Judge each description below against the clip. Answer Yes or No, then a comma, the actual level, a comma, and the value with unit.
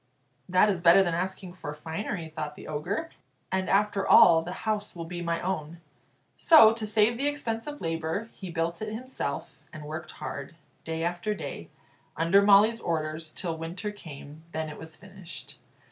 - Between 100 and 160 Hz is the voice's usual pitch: No, medium, 175 Hz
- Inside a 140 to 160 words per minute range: No, average, 175 wpm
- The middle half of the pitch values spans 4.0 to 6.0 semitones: Yes, average, 4.3 semitones